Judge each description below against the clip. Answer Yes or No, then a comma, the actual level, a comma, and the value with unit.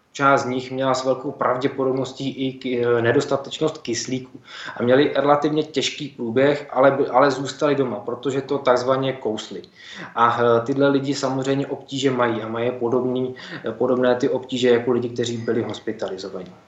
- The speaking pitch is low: Yes, low, 130 Hz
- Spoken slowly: No, average, 145 wpm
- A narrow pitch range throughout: Yes, narrow, 2.1 semitones